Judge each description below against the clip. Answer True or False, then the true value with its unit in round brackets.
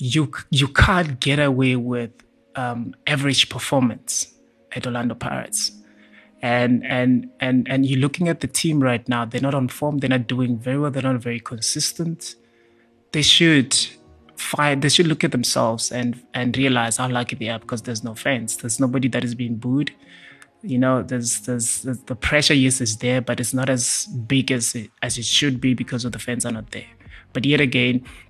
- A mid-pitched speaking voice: False (125 Hz)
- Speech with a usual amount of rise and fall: False (2.2 semitones)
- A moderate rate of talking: True (195 wpm)